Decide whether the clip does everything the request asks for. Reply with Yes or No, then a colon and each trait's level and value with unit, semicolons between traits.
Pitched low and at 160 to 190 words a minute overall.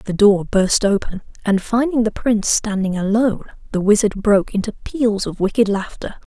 No: high, 210 Hz; average, 170 wpm